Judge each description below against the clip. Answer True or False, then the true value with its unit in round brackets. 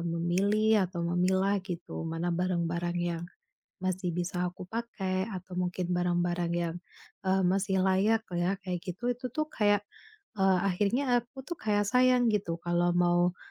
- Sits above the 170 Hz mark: True (185 Hz)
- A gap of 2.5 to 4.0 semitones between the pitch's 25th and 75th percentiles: True (2.9 semitones)